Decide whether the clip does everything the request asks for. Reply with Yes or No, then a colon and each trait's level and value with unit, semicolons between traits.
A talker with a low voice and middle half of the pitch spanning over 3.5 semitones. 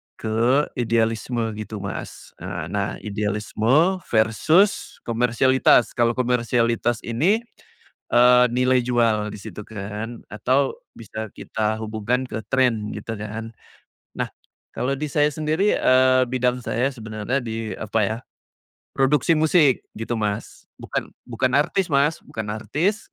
No: low, 120 Hz; average, 3.2 semitones